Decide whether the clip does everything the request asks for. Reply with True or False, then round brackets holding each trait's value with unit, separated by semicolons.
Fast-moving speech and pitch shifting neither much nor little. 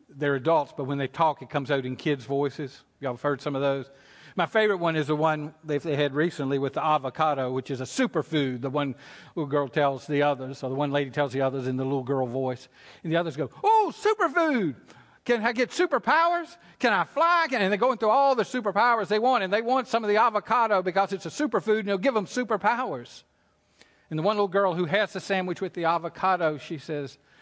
False (230 wpm; 7.1 semitones)